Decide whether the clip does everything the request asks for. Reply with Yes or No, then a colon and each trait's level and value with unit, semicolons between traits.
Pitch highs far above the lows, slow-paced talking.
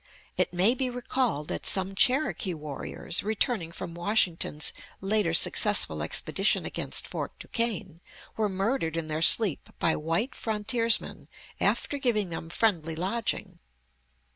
Yes: wide, 5.7 semitones; slow, 125 wpm